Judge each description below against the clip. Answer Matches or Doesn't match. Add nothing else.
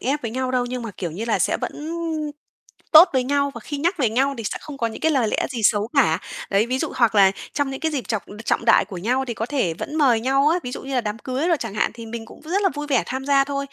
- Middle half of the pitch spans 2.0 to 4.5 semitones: Matches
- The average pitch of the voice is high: Matches